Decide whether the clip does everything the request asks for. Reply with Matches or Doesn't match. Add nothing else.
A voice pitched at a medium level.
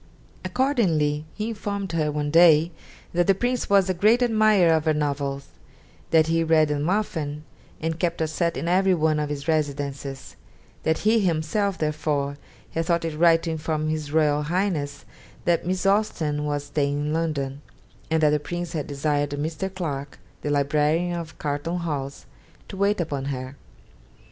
Matches